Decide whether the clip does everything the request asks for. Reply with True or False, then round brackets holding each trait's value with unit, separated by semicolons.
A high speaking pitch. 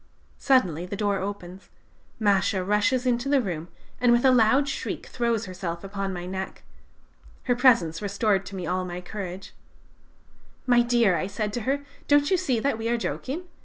True (210 Hz)